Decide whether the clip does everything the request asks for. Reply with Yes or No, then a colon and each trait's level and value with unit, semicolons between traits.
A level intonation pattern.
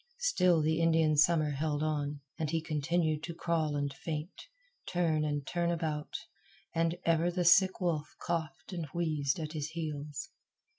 Yes: narrow, 2.2 semitones